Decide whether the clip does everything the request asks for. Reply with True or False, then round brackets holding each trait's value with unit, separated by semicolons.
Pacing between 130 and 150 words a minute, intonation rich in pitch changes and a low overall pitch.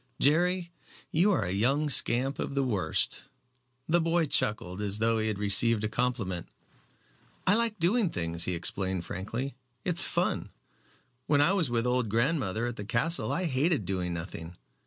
False (165 wpm; 8.3 semitones; 120 Hz)